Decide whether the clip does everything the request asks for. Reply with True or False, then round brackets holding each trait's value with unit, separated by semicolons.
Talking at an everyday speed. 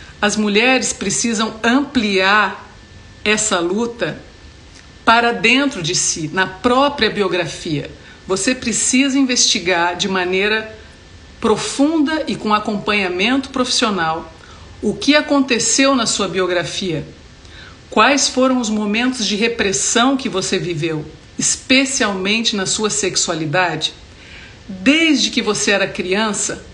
False (105 wpm)